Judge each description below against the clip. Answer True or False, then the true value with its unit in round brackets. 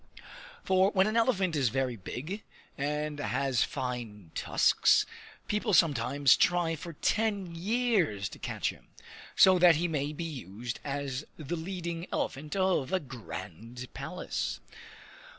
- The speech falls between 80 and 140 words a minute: True (135 wpm)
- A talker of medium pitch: True (150 Hz)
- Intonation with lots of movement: True (6.5 semitones)